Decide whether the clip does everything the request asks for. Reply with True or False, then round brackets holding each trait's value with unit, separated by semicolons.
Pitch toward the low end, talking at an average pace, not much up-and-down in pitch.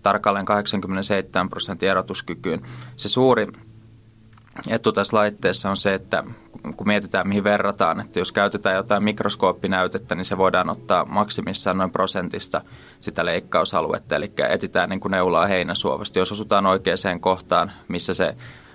True (100 Hz; 135 wpm; 2.2 semitones)